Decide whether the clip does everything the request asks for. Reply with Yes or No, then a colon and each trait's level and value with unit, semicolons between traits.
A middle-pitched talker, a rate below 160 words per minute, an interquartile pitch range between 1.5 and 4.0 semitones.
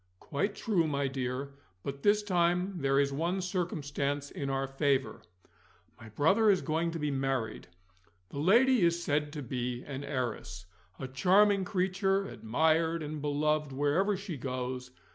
No: medium, 150 Hz; average, 150 wpm; average, 4.9 semitones